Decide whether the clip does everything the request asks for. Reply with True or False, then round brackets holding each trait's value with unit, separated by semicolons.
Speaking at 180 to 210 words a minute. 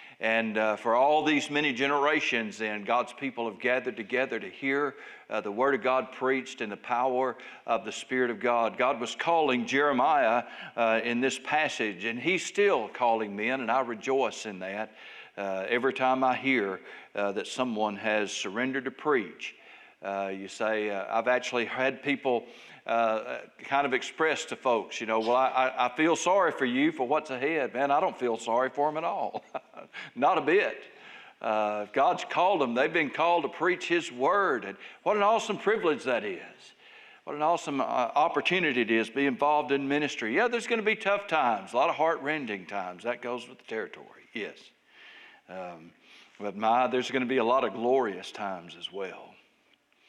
True (190 wpm)